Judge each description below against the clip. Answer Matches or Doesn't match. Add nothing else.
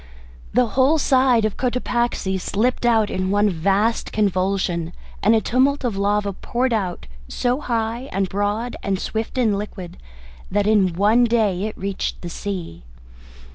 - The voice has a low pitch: Doesn't match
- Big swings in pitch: Doesn't match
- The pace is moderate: Matches